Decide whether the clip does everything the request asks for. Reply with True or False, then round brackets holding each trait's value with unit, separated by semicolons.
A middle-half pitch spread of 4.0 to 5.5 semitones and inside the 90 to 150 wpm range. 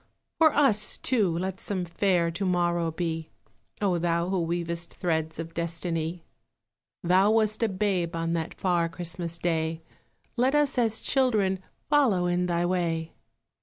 False (3.2 semitones; 145 wpm)